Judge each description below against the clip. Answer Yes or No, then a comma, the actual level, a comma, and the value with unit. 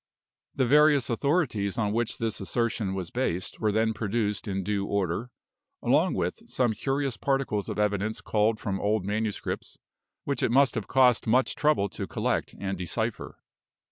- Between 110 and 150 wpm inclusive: No, average, 160 wpm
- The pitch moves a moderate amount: Yes, average, 3.5 semitones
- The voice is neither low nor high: No, low, 110 Hz